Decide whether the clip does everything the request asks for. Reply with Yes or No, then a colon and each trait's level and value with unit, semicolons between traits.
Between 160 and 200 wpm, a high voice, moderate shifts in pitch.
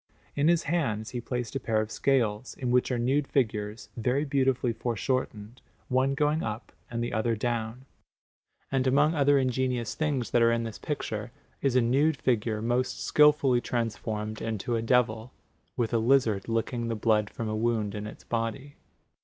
No: average, 175 wpm; low, 120 Hz; average, 3.1 semitones